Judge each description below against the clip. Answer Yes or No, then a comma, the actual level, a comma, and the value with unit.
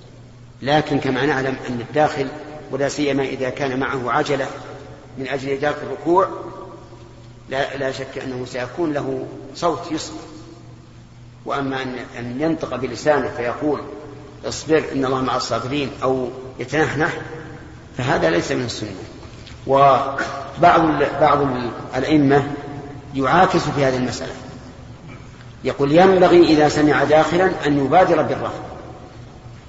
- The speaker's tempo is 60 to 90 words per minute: No, average, 110 wpm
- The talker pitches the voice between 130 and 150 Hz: Yes, medium, 140 Hz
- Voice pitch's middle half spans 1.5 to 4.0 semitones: Yes, narrow, 2.6 semitones